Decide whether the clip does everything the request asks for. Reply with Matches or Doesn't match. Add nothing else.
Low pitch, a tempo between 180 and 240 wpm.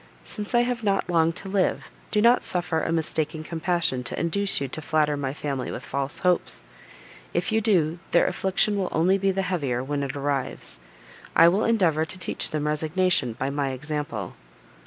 Doesn't match